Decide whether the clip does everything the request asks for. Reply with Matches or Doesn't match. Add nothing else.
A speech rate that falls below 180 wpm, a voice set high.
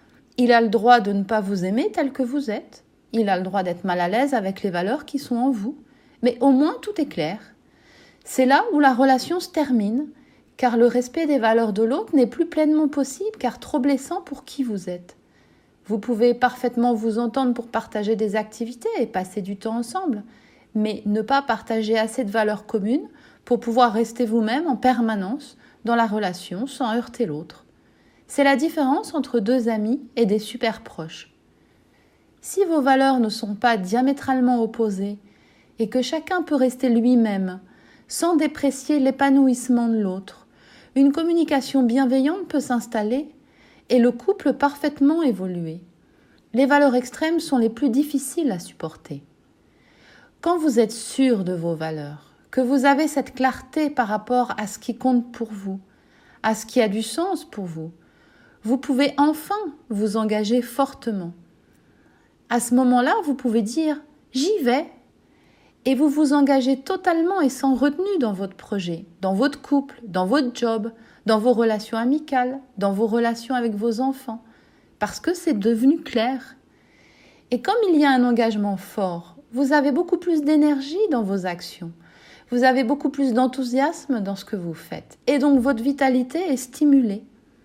Matches